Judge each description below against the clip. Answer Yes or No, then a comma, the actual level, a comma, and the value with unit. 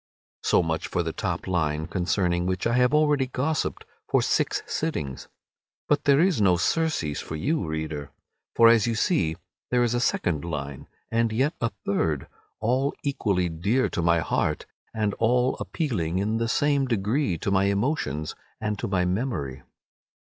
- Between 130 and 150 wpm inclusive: No, average, 165 wpm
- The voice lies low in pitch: Yes, low, 105 Hz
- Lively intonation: Yes, wide, 7.4 semitones